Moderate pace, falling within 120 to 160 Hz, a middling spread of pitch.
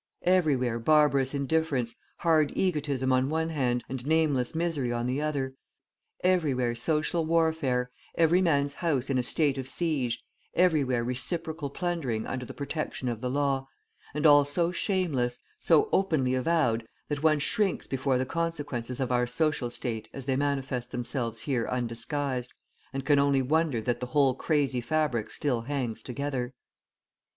Yes: average, 150 wpm; medium, 140 Hz; average, 3.9 semitones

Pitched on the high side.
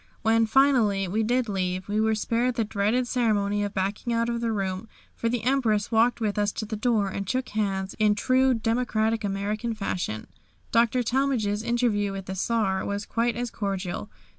Yes: high, 220 Hz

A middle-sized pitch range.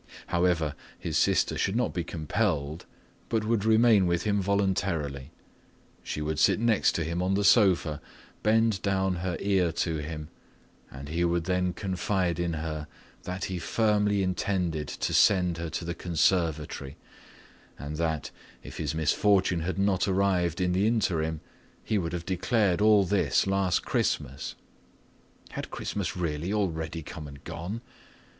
Yes: average, 3.5 semitones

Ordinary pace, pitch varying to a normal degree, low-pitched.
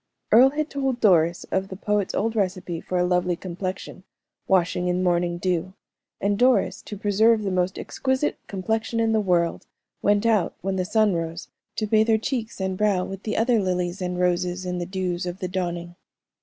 No: average, 190 wpm; average, 3.3 semitones; high, 190 Hz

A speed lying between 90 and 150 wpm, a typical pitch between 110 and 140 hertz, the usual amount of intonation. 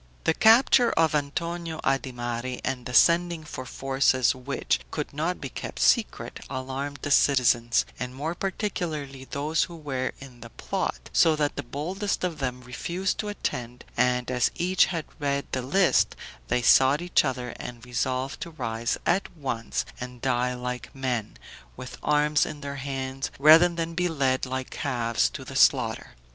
No: average, 165 wpm; low, 135 Hz; average, 4.3 semitones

